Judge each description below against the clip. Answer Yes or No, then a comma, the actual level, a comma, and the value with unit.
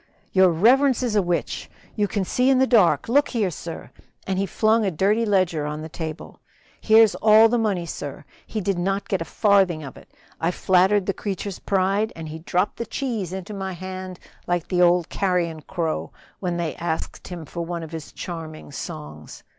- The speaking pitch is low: No, medium, 185 Hz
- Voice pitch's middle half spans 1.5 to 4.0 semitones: Yes, average, 3.7 semitones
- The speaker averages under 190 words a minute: No, average, 195 wpm